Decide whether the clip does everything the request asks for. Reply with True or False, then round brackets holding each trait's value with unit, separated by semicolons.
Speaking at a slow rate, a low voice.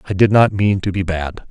False (280 wpm; 95 Hz)